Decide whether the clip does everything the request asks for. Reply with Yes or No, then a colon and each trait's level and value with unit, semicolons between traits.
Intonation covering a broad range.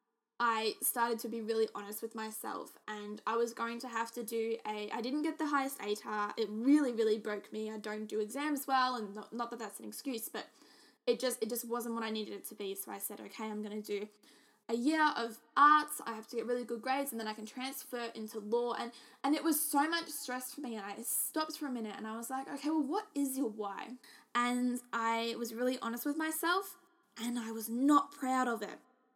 No: average, 3.3 semitones